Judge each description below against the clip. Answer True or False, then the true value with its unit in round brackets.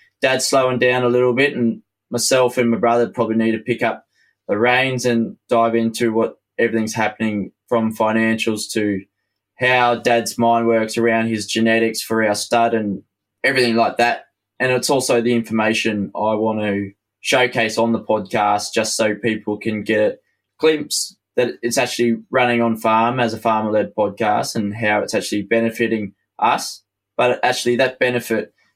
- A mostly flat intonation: True (1.8 semitones)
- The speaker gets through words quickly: False (170 wpm)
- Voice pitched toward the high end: False (115 Hz)